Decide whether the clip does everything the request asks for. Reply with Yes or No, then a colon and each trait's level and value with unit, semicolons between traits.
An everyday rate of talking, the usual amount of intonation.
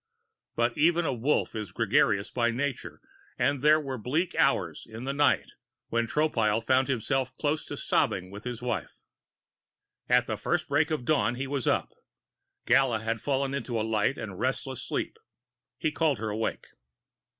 Yes: average, 165 wpm; average, 4.0 semitones